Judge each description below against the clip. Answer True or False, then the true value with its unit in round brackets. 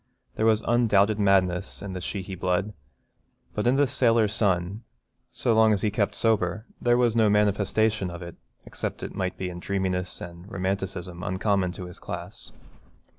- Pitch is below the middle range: True (100 Hz)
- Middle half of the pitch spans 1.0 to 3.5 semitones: True (3.1 semitones)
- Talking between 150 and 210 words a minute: True (175 wpm)